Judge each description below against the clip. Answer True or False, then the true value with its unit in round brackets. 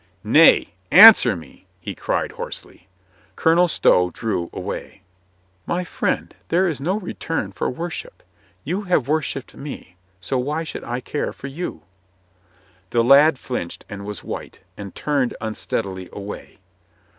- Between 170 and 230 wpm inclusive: False (145 wpm)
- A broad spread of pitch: True (8.7 semitones)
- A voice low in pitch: True (130 Hz)